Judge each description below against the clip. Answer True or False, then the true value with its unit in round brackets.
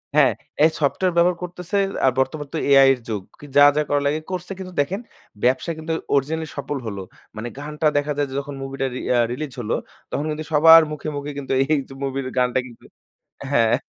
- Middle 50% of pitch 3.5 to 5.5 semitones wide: False (2.9 semitones)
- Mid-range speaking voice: True (145 Hz)